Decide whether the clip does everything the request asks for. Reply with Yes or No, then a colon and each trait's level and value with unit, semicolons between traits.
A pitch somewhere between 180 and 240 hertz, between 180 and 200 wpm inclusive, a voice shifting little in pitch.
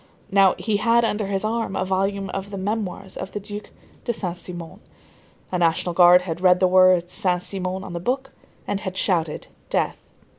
Yes: high, 190 Hz; average, 190 wpm; narrow, 2.2 semitones